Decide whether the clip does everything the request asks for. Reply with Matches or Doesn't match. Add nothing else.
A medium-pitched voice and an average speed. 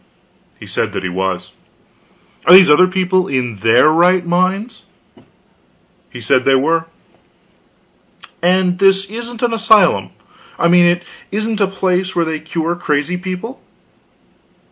Doesn't match